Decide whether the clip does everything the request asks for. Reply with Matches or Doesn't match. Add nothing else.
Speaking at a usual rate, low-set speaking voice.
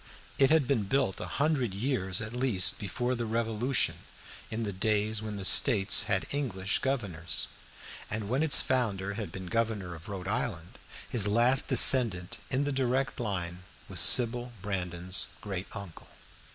Matches